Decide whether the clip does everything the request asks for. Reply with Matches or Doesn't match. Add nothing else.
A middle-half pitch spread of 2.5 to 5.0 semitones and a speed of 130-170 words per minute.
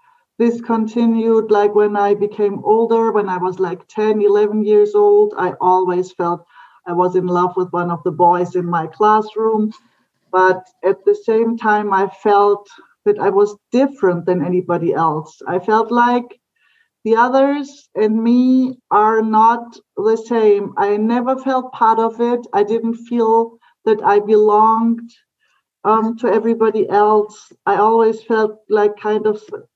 Matches